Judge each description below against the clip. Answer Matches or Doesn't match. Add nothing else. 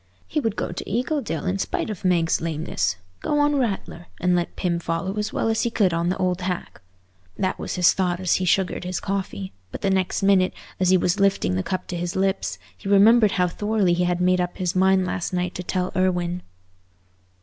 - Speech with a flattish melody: Matches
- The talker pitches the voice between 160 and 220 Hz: Matches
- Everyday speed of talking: Doesn't match